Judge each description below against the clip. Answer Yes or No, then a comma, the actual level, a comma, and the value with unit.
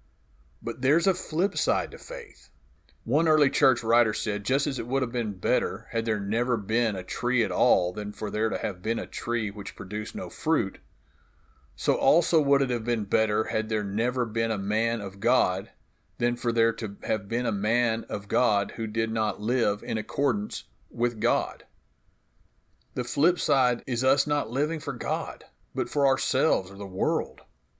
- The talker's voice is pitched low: Yes, low, 115 Hz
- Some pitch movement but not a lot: Yes, average, 3.7 semitones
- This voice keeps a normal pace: Yes, average, 190 wpm